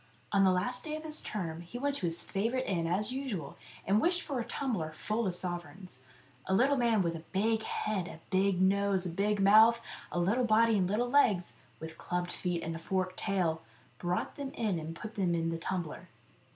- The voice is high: Yes, high, 195 Hz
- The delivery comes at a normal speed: No, fast, 210 wpm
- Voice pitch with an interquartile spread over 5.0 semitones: No, average, 4.6 semitones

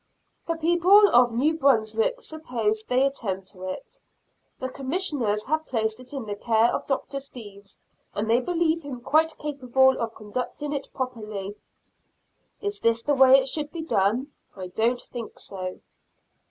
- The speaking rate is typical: Yes, average, 155 wpm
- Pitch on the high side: Yes, very high, 255 Hz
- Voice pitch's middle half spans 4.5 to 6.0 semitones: Yes, average, 5.2 semitones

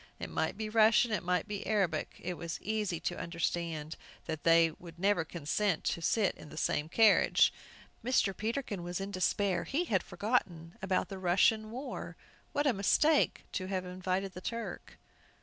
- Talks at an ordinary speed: Yes, average, 170 wpm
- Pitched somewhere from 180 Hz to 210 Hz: Yes, high, 190 Hz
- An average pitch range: Yes, average, 4.1 semitones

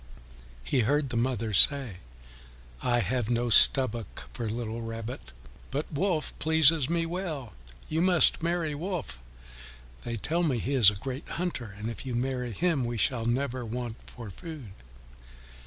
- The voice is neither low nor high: No, low, 125 Hz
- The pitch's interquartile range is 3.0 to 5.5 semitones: Yes, average, 5.1 semitones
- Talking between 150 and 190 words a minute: Yes, average, 155 wpm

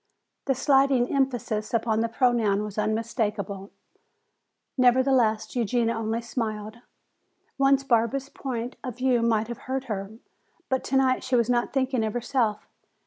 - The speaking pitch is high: Yes, high, 235 Hz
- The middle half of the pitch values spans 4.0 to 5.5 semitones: No, average, 3.0 semitones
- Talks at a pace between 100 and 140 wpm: Yes, slow, 135 wpm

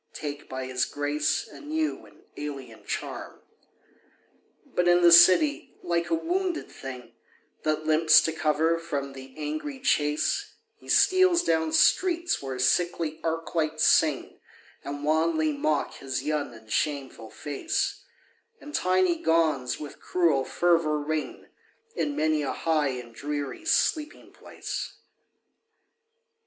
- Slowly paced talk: Yes, slow, 130 wpm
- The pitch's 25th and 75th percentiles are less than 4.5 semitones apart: Yes, average, 3.2 semitones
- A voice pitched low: No, medium, 155 Hz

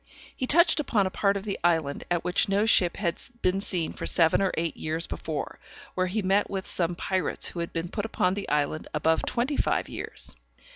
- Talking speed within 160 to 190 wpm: No, fast, 205 wpm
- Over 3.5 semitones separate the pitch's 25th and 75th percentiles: No, average, 3.2 semitones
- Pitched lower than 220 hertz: Yes, medium, 185 Hz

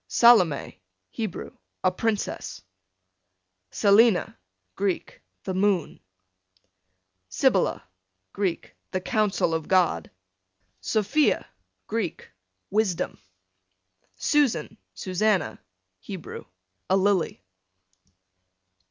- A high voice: Yes, high, 195 Hz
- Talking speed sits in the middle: No, slow, 70 wpm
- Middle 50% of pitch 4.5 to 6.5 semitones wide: No, average, 3.3 semitones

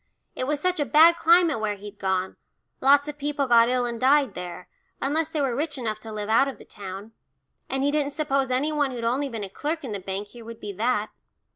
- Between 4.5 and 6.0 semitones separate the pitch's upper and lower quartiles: Yes, average, 5.3 semitones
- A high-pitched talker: Yes, very high, 255 Hz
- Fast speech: Yes, fast, 240 wpm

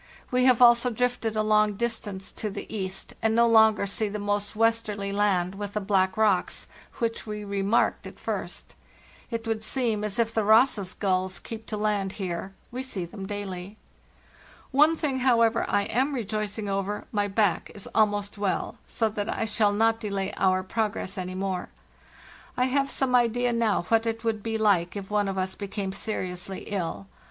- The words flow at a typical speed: Yes, average, 180 wpm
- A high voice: Yes, high, 210 Hz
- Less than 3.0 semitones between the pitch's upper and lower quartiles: Yes, narrow, 2.5 semitones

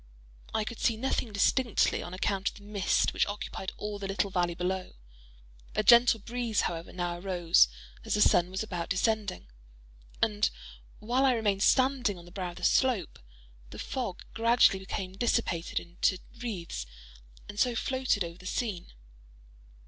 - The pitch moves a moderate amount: Yes, average, 4.2 semitones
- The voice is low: No, high, 200 Hz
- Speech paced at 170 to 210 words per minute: No, average, 160 wpm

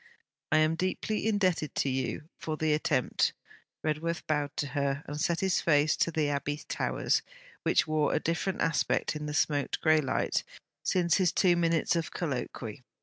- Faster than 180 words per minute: No, average, 170 wpm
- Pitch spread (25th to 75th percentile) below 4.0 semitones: Yes, narrow, 2.5 semitones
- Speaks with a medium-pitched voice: Yes, medium, 155 Hz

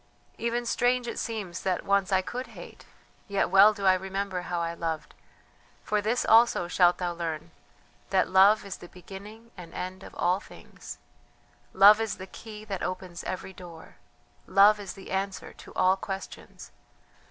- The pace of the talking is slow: No, average, 165 wpm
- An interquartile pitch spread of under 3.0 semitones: Yes, narrow, 2.6 semitones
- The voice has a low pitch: No, high, 195 Hz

